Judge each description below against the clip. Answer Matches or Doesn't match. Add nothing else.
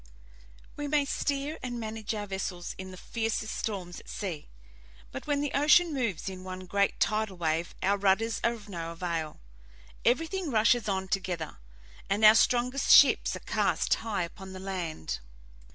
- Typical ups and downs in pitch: Matches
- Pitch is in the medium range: Doesn't match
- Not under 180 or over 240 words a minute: Doesn't match